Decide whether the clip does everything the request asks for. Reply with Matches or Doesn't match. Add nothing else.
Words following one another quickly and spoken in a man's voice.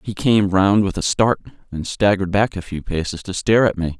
Matches